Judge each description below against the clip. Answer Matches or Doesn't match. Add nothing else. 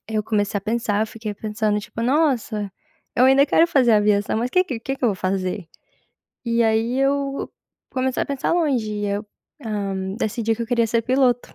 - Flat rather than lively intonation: Doesn't match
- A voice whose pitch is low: Doesn't match